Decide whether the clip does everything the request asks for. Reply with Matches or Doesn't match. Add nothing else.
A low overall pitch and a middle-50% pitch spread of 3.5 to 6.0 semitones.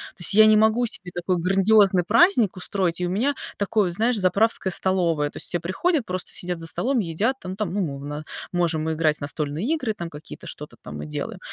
Doesn't match